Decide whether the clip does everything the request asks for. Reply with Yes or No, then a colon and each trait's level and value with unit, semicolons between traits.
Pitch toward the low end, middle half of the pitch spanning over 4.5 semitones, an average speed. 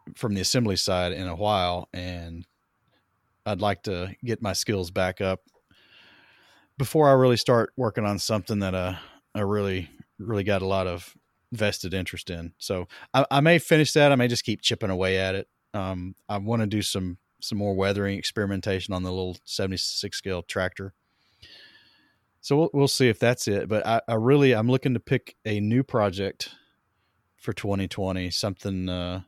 No: low, 100 Hz; average, 3.7 semitones; average, 180 wpm